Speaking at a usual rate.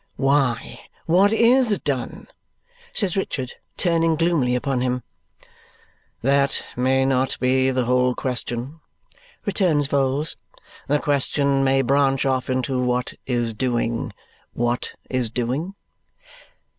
No: slow, 110 wpm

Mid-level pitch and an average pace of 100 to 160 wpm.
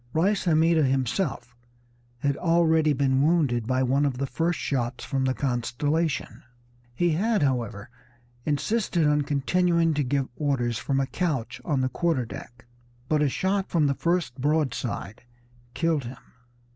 Yes: medium, 145 Hz; average, 145 wpm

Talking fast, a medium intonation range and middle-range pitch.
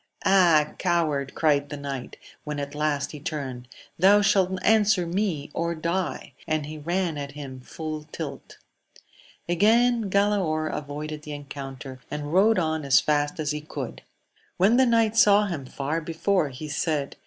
No: average, 165 wpm; average, 4.5 semitones; medium, 155 Hz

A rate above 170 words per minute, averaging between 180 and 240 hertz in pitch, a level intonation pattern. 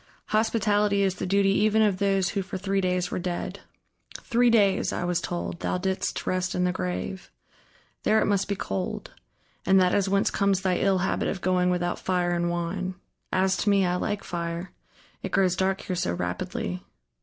Yes: average, 190 wpm; high, 190 Hz; narrow, 1.8 semitones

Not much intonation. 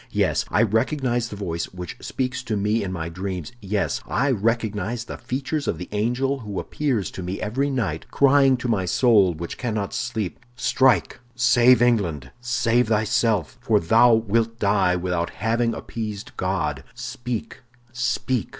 No: average, 4.0 semitones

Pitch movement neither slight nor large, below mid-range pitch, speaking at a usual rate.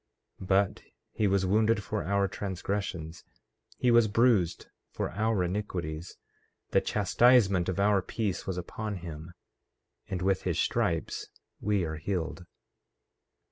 No: average, 3.0 semitones; very low, 95 Hz; slow, 130 wpm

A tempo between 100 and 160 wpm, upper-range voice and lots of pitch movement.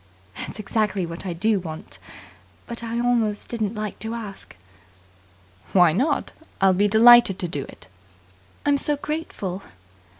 No: average, 140 wpm; high, 215 Hz; average, 3.9 semitones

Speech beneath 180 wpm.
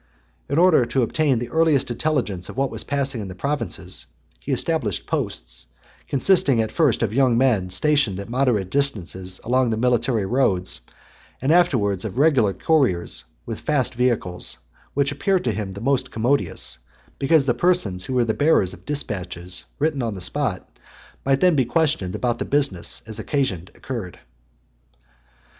Yes: average, 160 wpm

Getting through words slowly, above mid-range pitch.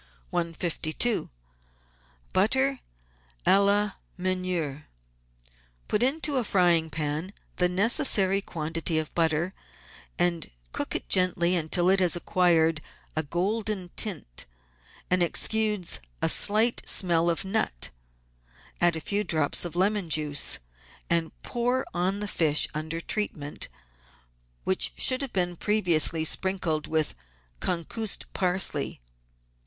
No: slow, 115 wpm; medium, 180 Hz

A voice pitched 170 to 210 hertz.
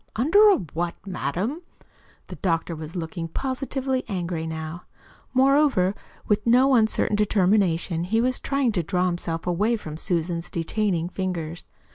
Yes: medium, 185 Hz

